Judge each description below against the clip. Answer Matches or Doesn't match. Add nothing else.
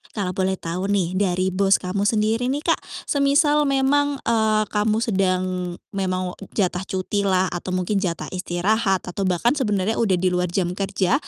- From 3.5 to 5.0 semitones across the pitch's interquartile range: Doesn't match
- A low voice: Doesn't match